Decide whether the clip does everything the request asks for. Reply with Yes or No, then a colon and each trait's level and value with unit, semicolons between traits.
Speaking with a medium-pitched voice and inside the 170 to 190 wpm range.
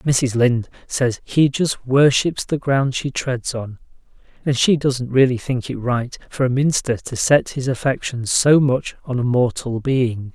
No: low, 130 Hz; average, 180 wpm